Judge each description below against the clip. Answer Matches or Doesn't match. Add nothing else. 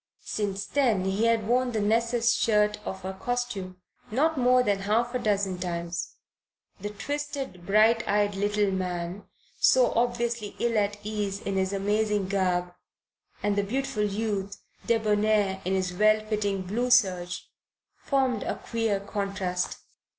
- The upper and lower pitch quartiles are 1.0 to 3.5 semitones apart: Matches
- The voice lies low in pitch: Doesn't match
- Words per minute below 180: Matches